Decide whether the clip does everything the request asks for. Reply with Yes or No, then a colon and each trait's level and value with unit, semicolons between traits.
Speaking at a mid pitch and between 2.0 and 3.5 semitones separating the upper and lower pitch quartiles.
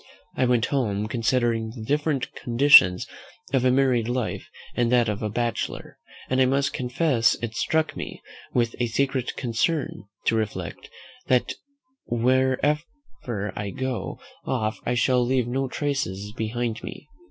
No: low, 125 Hz; average, 2.7 semitones